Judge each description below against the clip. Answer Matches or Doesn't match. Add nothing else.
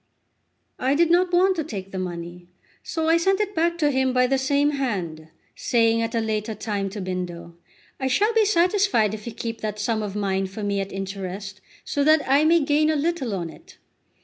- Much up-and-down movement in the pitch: Matches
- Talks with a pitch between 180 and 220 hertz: Doesn't match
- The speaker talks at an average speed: Doesn't match